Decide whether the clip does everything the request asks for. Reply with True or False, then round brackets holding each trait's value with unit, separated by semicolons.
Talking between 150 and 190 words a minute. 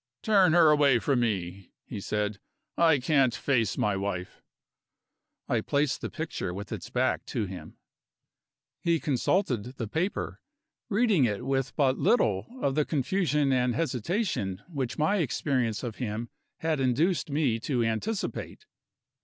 False (140 wpm)